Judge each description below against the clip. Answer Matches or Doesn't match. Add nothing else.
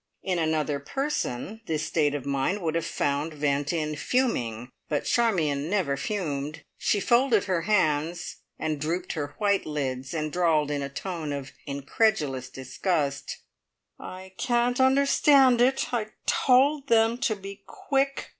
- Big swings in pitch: Matches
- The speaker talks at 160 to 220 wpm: Doesn't match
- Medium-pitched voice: Matches